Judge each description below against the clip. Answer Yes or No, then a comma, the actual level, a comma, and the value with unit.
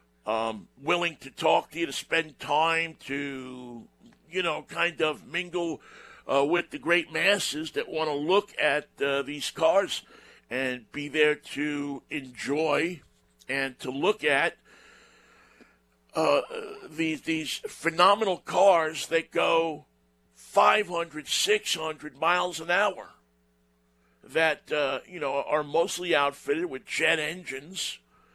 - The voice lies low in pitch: No, medium, 150 Hz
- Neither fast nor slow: No, slow, 125 wpm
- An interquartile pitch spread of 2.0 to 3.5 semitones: No, average, 4.1 semitones